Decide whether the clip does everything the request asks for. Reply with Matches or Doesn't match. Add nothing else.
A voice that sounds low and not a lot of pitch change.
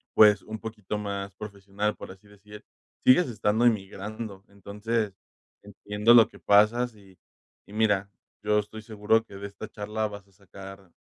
Matches